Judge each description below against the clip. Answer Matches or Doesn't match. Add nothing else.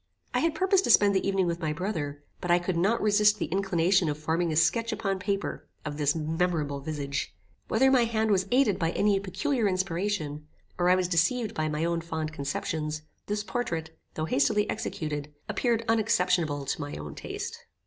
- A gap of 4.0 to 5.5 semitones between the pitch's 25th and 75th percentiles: Matches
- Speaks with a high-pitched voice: Doesn't match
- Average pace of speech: Matches